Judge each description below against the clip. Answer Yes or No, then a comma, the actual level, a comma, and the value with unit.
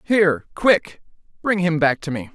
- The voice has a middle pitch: Yes, medium, 165 Hz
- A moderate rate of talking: Yes, average, 180 wpm